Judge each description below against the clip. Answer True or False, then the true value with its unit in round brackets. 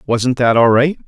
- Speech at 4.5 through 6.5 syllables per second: True (4.7 syllables/s)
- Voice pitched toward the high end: False (125 Hz)